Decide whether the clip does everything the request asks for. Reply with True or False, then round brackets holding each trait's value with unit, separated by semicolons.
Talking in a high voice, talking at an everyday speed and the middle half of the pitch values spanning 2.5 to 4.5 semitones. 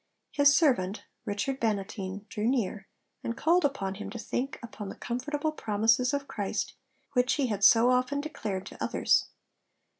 False (235 Hz; 155 wpm; 5.2 semitones)